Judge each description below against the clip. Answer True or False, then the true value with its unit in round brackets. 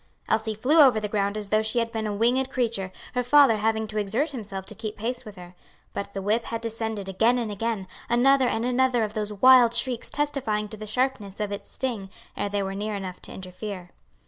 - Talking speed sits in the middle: False (225 wpm)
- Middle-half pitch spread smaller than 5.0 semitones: True (3.1 semitones)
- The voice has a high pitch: True (220 Hz)